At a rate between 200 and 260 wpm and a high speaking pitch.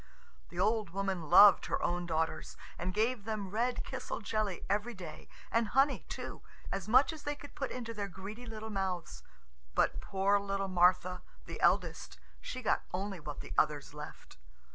No: average, 170 wpm; high, 200 Hz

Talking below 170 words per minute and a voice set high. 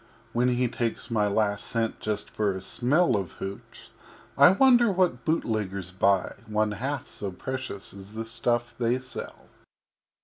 No: average, 150 wpm; low, 115 Hz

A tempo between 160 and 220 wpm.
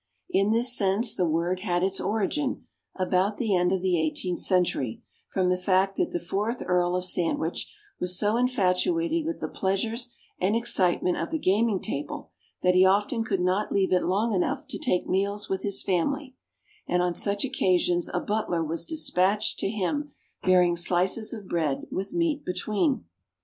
Yes: average, 175 wpm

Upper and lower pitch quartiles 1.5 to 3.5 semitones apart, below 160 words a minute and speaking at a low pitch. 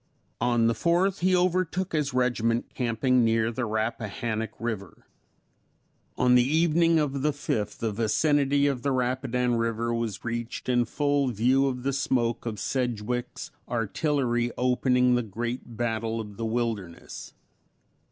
Yes: average, 3.1 semitones; average, 140 wpm; low, 120 Hz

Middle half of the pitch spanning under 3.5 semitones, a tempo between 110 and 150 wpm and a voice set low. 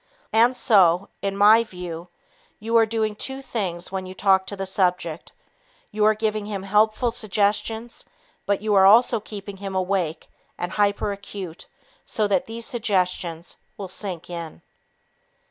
No: average, 2.7 semitones; average, 145 wpm; high, 200 Hz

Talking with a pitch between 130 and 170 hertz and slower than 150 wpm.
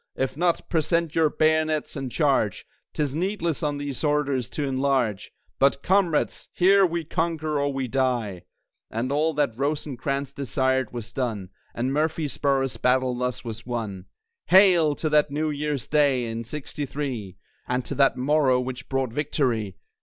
No: medium, 140 Hz; average, 155 wpm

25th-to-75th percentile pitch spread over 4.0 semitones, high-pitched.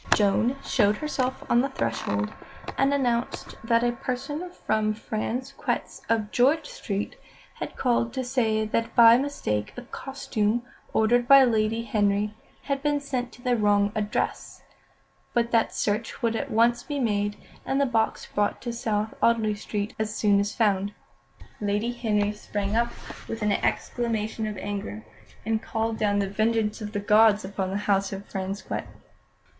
No: average, 2.7 semitones; high, 220 Hz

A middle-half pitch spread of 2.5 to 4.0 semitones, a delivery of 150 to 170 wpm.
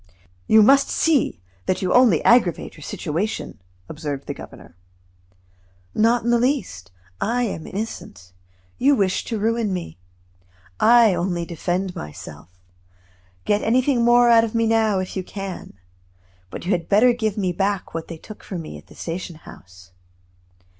No: wide, 5.4 semitones; average, 155 wpm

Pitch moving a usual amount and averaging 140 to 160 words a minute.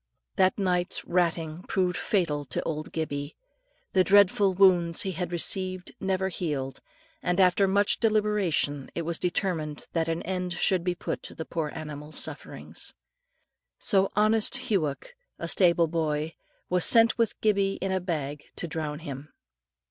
Yes: average, 3.4 semitones; average, 150 wpm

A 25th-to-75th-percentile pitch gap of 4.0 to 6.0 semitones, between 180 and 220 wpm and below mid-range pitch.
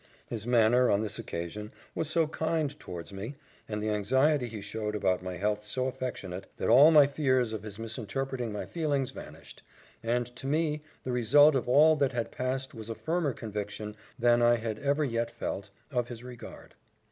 Yes: average, 4.5 semitones; average, 185 wpm; low, 120 Hz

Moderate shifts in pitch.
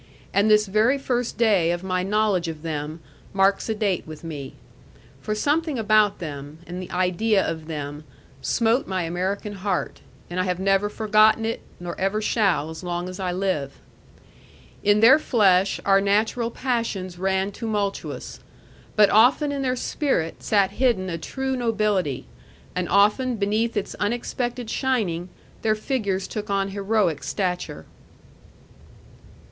Yes: average, 3.7 semitones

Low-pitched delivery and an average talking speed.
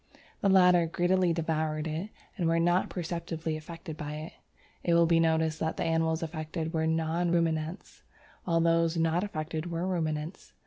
No: medium, 165 Hz; average, 165 wpm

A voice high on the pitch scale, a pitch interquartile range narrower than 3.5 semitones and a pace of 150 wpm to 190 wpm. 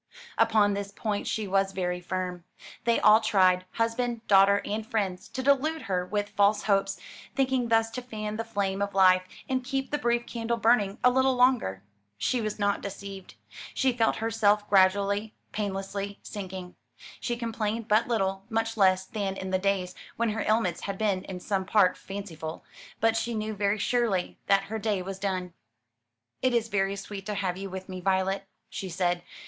Yes: high, 205 Hz; average, 2.8 semitones; average, 180 wpm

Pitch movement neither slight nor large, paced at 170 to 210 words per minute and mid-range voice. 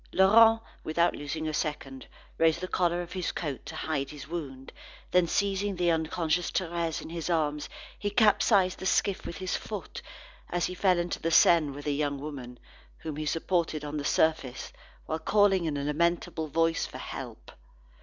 Yes: average, 3.2 semitones; average, 180 wpm; medium, 165 Hz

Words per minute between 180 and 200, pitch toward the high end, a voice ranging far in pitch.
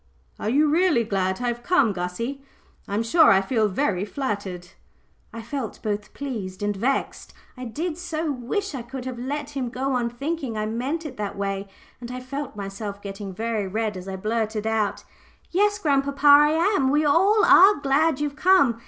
Yes: average, 185 wpm; high, 245 Hz; wide, 5.8 semitones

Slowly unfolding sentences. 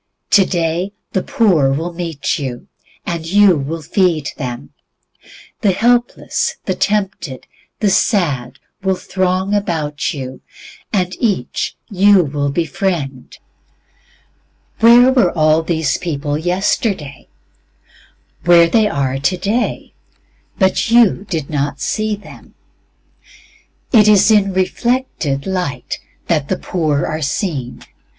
Yes: slow, 110 wpm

